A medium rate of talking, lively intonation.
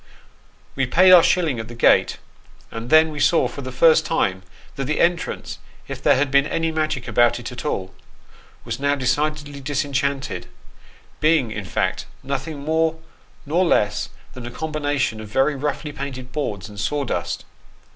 No: average, 175 wpm; average, 3.7 semitones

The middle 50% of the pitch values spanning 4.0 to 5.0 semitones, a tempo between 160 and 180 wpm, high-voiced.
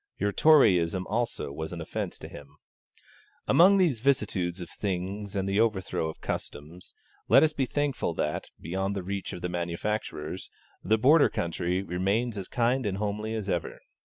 No: average, 4.3 semitones; average, 165 wpm; low, 100 Hz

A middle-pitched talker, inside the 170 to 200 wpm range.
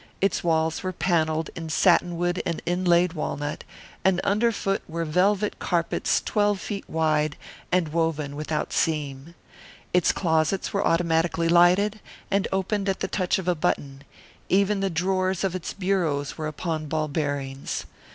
No: medium, 170 Hz; average, 150 wpm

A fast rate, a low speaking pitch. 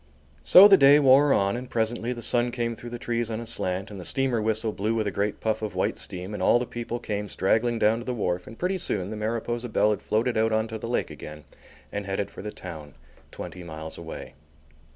Yes: fast, 240 wpm; low, 110 Hz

